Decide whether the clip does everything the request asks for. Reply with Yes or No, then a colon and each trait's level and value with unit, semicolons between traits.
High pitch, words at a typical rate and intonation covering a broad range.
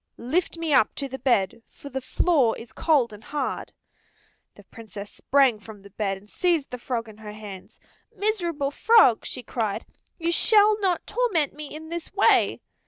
Yes: very high, 270 Hz; average, 175 wpm; wide, 7.4 semitones